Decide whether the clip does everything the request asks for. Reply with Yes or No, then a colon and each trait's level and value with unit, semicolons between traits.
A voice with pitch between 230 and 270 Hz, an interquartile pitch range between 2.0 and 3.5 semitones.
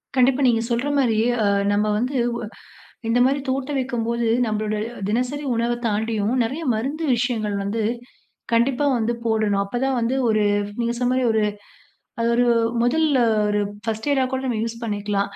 Yes: high, 235 Hz; average, 3.0 semitones